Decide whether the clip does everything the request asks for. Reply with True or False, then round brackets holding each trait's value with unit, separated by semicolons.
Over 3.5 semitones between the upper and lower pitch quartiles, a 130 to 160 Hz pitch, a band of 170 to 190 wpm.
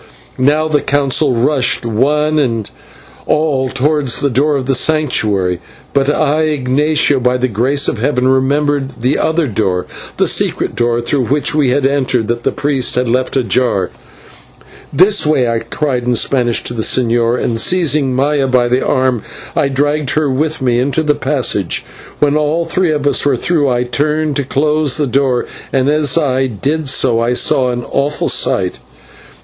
False (3.2 semitones; 135 Hz; 175 wpm)